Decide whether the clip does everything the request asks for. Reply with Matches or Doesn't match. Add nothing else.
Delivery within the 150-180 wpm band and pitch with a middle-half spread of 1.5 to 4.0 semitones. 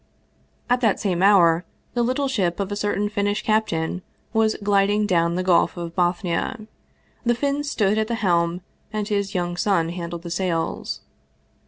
Matches